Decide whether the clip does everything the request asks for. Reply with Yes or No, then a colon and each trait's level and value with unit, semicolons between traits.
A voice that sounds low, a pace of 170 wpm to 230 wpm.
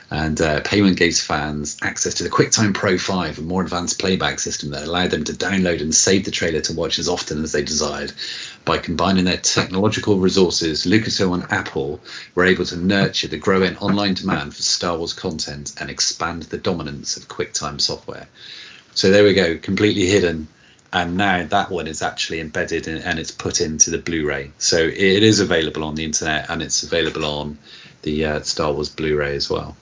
Yes: very low, 85 Hz; average, 195 wpm